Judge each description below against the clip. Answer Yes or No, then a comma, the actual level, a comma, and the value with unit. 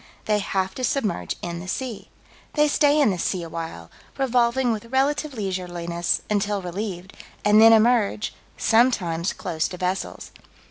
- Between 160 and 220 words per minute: No, average, 145 wpm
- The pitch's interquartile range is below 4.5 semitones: No, average, 5.3 semitones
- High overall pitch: Yes, high, 205 Hz